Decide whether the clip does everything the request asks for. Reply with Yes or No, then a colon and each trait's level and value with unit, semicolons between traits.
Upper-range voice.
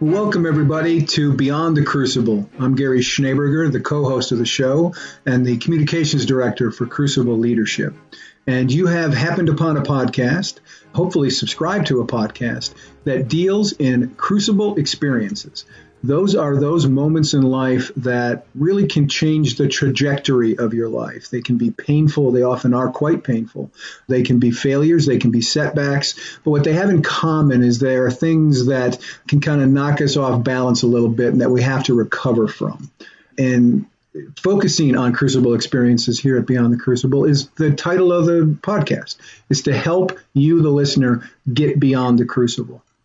No: low, 135 Hz